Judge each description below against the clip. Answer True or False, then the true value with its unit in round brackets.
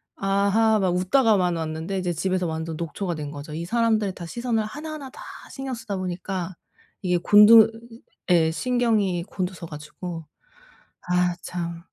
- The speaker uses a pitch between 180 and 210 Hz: True (185 Hz)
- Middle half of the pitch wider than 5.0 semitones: False (4.2 semitones)